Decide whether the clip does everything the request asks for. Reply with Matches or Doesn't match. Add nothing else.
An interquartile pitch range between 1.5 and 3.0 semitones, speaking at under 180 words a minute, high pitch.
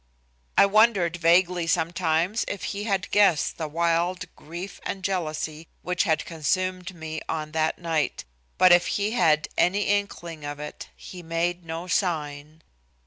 Doesn't match